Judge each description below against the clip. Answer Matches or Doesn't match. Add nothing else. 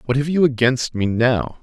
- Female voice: Doesn't match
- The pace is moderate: Doesn't match